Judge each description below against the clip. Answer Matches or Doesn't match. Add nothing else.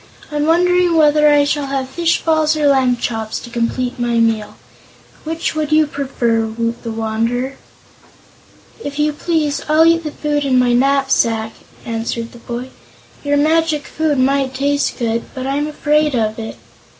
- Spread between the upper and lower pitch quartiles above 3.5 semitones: Matches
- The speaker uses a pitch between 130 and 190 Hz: Doesn't match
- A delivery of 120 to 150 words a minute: Doesn't match